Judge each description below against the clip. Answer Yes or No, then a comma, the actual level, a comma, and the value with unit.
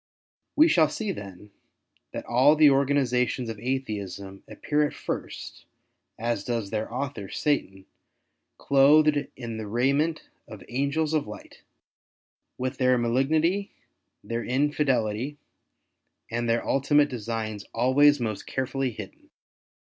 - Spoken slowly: Yes, slow, 115 wpm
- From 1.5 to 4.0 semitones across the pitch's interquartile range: No, average, 4.4 semitones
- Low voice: Yes, low, 130 Hz